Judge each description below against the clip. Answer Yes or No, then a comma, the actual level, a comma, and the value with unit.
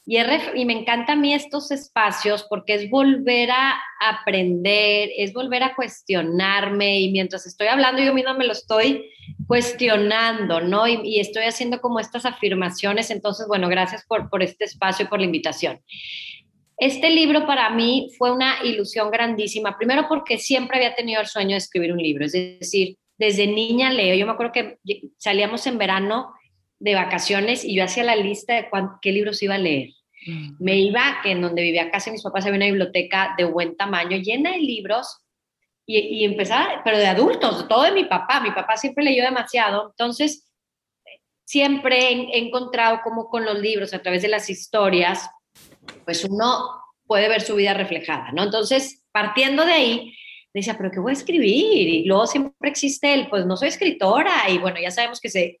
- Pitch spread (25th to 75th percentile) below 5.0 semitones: Yes, average, 4.3 semitones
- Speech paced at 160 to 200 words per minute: Yes, average, 185 wpm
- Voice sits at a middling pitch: No, high, 215 Hz